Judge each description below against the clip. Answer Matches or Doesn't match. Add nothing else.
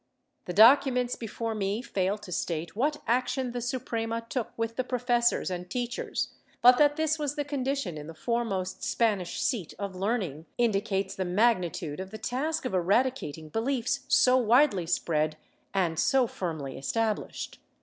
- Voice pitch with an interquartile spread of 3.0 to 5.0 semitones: Doesn't match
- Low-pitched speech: Doesn't match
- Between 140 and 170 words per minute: Matches